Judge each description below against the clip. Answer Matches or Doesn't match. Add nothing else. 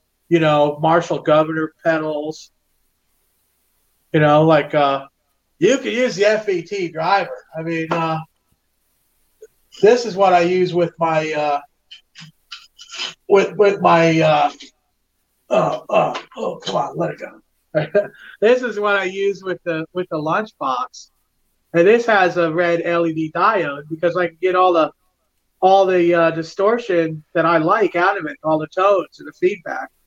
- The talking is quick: Doesn't match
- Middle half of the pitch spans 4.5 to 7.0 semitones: Doesn't match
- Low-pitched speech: Doesn't match